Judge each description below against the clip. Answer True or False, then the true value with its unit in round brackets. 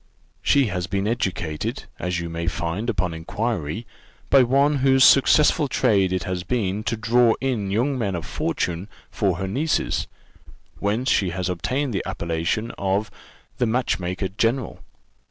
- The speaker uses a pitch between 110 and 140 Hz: False (100 Hz)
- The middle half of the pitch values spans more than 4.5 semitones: True (5.5 semitones)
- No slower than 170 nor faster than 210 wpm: False (155 wpm)